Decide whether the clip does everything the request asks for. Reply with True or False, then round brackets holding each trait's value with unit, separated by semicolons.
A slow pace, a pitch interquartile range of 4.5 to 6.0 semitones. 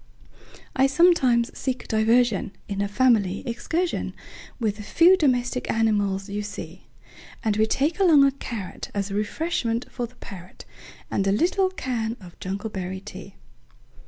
True (120 wpm; 4.8 semitones)